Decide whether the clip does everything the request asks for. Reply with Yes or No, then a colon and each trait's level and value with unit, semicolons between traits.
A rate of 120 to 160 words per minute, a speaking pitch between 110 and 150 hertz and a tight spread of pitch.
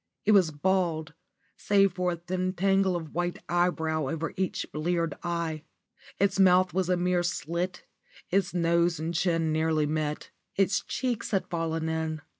No: average, 155 wpm; medium, 175 Hz; narrow, 2.3 semitones